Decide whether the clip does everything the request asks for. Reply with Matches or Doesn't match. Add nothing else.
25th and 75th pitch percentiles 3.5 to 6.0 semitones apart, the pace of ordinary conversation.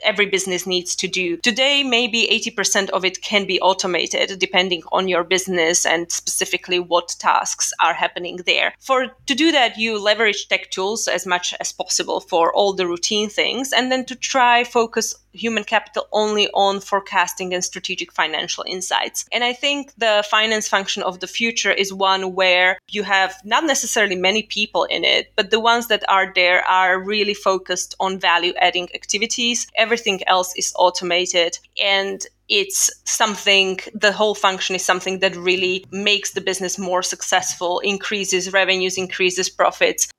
Doesn't match